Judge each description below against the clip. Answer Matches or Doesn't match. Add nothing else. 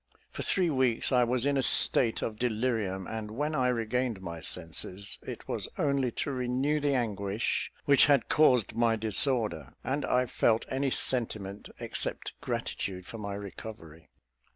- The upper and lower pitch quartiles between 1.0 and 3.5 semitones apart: Doesn't match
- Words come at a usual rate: Matches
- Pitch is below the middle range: Matches